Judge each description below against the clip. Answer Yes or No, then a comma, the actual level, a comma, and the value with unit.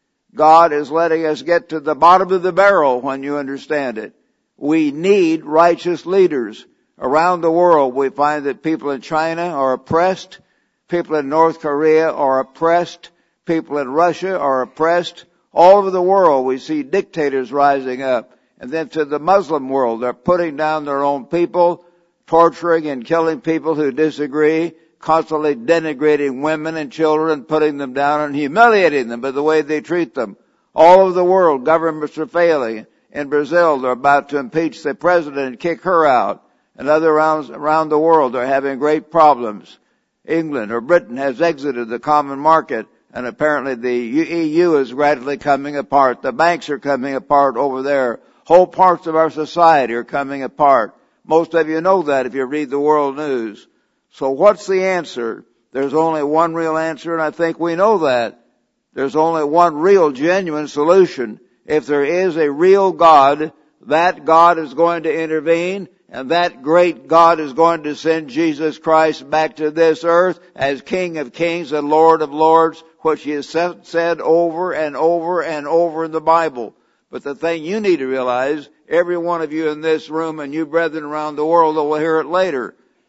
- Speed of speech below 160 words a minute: No, average, 180 wpm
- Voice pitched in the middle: Yes, medium, 160 Hz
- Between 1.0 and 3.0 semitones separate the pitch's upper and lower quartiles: Yes, narrow, 2.6 semitones